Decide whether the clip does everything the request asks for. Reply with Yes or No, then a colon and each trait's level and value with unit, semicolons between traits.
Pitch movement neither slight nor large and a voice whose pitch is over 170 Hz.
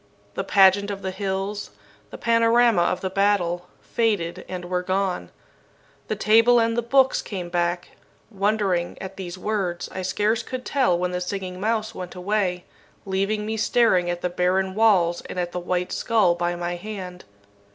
Yes: average, 3.1 semitones; high, 190 Hz